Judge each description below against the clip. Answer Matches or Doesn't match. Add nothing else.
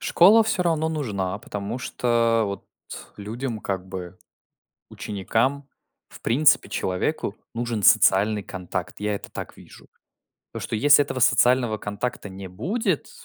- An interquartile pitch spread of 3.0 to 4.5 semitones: Doesn't match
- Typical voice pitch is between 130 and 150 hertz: Doesn't match